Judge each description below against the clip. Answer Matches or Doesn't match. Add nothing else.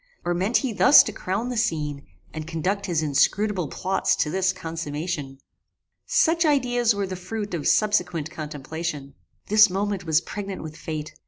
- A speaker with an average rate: Matches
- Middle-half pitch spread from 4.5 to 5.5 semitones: Matches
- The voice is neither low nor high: Matches